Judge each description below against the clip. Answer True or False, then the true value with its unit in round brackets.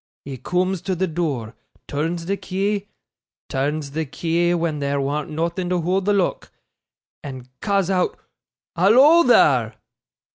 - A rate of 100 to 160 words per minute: True (140 wpm)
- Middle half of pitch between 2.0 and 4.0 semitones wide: False (4.8 semitones)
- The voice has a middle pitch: True (170 Hz)